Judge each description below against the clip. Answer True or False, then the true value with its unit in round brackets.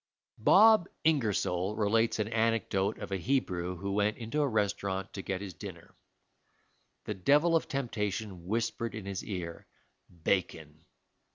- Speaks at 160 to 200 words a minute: False (140 wpm)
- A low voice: True (105 Hz)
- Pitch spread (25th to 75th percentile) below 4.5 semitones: True (3.3 semitones)